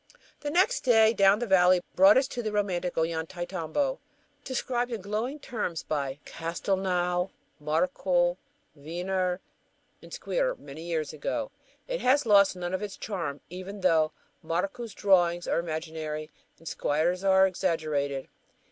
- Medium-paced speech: No, slow, 130 wpm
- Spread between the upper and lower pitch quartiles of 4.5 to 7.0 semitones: Yes, average, 4.8 semitones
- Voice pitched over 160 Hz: Yes, medium, 185 Hz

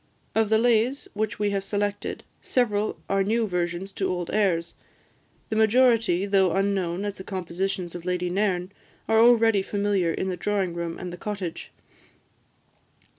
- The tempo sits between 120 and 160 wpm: Yes, average, 155 wpm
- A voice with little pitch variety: No, average, 3.0 semitones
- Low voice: No, high, 195 Hz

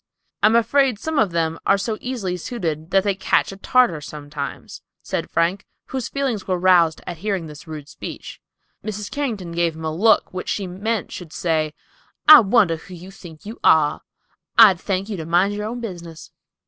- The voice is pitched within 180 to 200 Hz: Yes, medium, 185 Hz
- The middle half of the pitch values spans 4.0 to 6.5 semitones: Yes, average, 4.6 semitones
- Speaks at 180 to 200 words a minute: Yes, average, 190 wpm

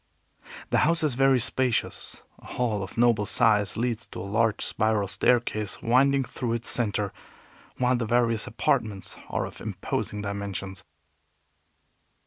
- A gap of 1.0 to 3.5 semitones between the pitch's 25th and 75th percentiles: Yes, average, 3.2 semitones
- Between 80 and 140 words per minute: Yes, slow, 135 wpm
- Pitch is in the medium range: No, low, 115 Hz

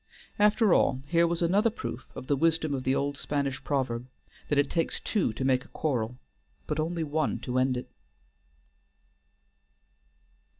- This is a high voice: No, medium, 145 Hz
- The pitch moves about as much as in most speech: Yes, average, 4.2 semitones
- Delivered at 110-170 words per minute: Yes, average, 160 wpm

